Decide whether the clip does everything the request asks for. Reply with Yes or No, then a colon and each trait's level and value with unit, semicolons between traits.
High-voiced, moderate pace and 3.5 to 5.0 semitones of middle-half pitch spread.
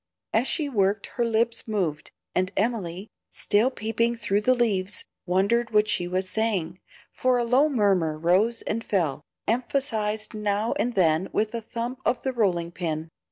Yes: high, 215 Hz; average, 160 wpm; average, 4.1 semitones